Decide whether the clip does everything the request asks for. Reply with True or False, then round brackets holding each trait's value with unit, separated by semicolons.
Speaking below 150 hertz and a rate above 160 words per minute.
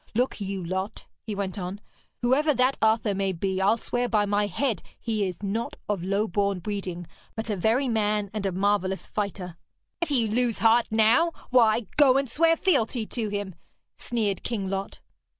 False (210 Hz; 180 wpm)